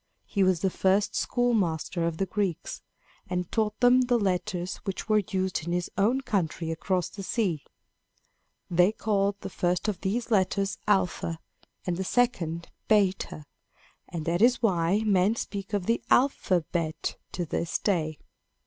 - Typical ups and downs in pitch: Yes, average, 3.4 semitones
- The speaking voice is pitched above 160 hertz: Yes, high, 190 Hz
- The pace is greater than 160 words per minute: No, average, 150 wpm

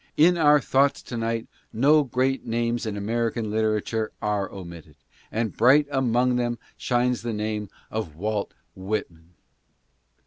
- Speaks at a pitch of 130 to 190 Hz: No, low, 115 Hz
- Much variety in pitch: No, average, 2.9 semitones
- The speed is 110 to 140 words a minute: Yes, slow, 135 wpm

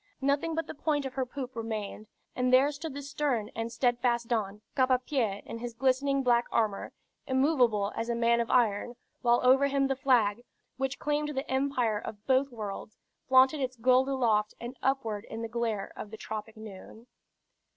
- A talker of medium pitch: No, high, 245 Hz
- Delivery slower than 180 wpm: No, average, 185 wpm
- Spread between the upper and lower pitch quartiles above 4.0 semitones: No, average, 3.2 semitones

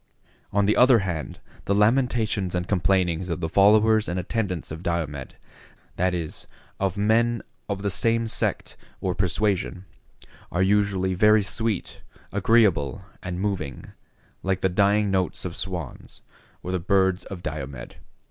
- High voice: No, very low, 95 Hz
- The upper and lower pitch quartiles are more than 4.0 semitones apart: No, average, 2.8 semitones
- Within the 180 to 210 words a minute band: No, average, 140 wpm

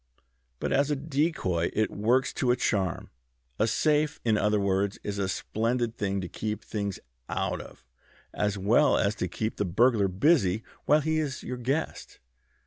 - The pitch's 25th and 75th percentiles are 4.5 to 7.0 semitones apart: Yes, average, 5.1 semitones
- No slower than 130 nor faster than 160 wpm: No, average, 170 wpm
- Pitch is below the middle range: Yes, low, 110 Hz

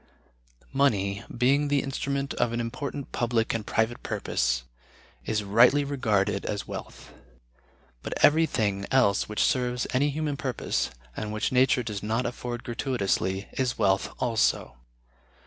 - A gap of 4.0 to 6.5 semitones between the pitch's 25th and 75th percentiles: Yes, average, 4.4 semitones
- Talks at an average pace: No, slow, 130 wpm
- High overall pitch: No, low, 120 Hz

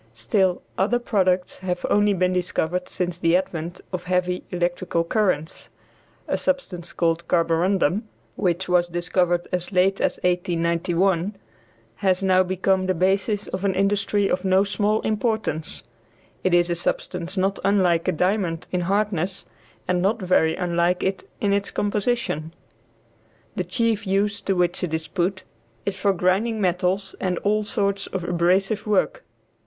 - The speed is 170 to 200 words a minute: No, average, 150 wpm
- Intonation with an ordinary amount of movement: No, narrow, 2.2 semitones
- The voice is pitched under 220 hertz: Yes, medium, 185 Hz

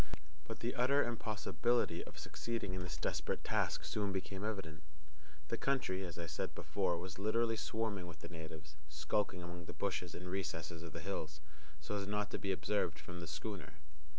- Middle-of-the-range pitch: No, very low, 95 Hz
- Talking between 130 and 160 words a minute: No, average, 180 wpm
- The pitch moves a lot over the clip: No, average, 4.2 semitones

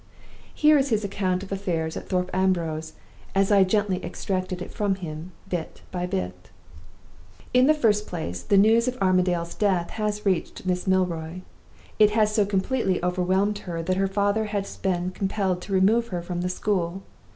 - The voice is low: No, high, 190 Hz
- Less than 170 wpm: No, average, 175 wpm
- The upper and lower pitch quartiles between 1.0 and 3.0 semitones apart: Yes, narrow, 2.5 semitones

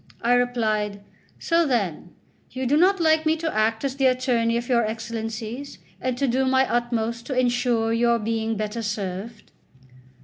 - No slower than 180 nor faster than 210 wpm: No, average, 165 wpm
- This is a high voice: Yes, high, 235 Hz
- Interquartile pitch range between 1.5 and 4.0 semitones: Yes, average, 2.8 semitones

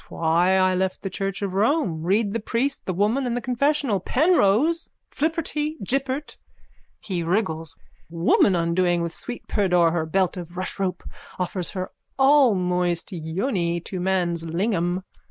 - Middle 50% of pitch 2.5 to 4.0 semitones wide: No, wide, 5.6 semitones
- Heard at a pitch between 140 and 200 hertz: Yes, high, 190 Hz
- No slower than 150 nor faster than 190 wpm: No, average, 140 wpm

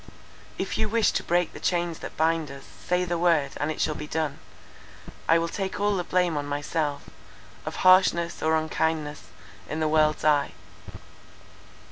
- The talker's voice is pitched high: No, medium, 160 Hz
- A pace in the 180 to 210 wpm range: No, average, 165 wpm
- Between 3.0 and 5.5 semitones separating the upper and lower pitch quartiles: No, narrow, 2.5 semitones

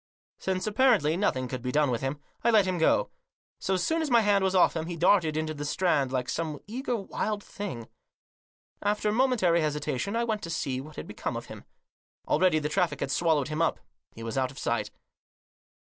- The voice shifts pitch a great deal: Yes, wide, 5.8 semitones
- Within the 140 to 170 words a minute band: No, fast, 205 wpm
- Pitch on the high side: No, medium, 170 Hz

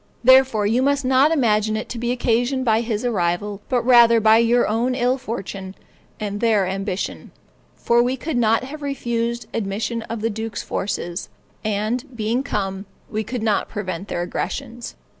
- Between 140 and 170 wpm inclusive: Yes, average, 165 wpm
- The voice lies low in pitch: No, high, 230 Hz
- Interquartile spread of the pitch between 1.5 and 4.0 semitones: Yes, average, 2.9 semitones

